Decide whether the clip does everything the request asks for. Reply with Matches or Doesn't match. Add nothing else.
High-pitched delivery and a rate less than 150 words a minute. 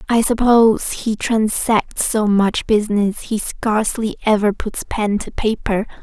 Matches